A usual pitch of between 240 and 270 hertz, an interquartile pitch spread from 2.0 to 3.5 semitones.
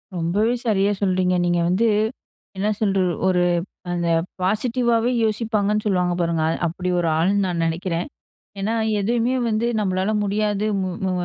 No: high, 195 Hz; average, 3.1 semitones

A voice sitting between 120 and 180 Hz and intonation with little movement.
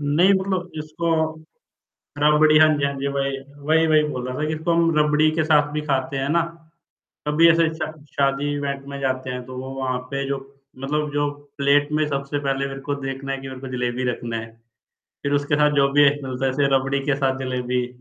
Yes: medium, 140 Hz; narrow, 2.1 semitones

